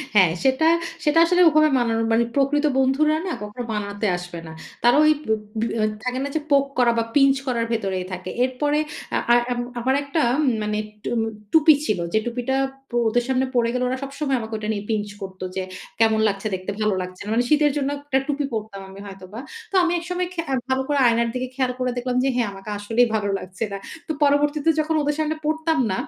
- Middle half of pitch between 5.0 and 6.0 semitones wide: Yes, average, 5.3 semitones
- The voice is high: Yes, high, 245 Hz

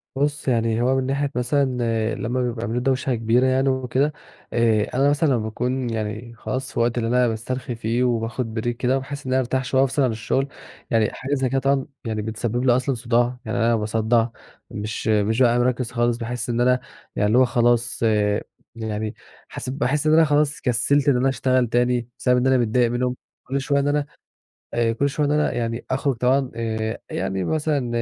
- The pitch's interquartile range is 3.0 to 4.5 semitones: No, narrow, 2.5 semitones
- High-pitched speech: No, low, 125 Hz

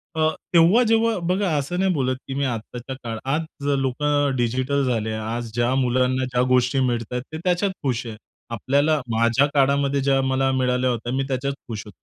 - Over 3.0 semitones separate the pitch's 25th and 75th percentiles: No, average, 2.7 semitones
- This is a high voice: No, low, 130 Hz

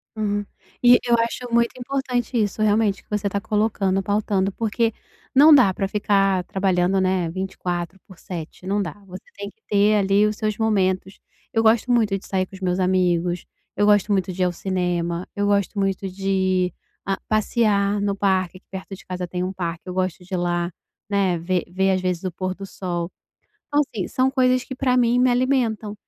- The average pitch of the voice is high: Yes, high, 195 Hz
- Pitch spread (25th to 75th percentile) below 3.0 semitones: Yes, narrow, 2.6 semitones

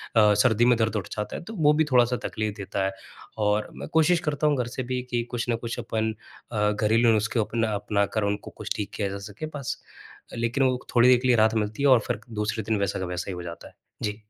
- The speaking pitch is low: Yes, low, 110 Hz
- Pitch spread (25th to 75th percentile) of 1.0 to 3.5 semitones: Yes, average, 3.1 semitones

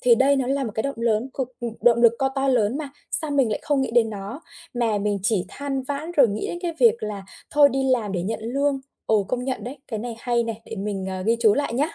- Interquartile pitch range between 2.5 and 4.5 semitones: Yes, average, 3.8 semitones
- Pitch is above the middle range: Yes, high, 240 Hz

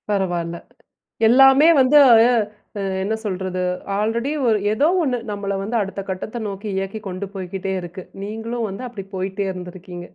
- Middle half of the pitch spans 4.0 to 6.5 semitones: No, average, 3.2 semitones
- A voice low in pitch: No, high, 200 Hz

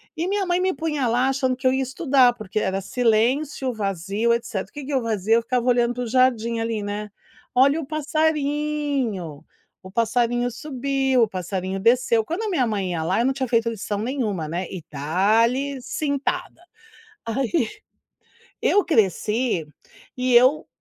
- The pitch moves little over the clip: No, average, 4.3 semitones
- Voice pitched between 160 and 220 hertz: No, high, 245 Hz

